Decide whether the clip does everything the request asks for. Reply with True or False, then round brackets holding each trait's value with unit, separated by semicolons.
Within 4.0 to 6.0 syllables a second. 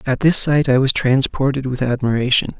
True (5.3 syllables/s)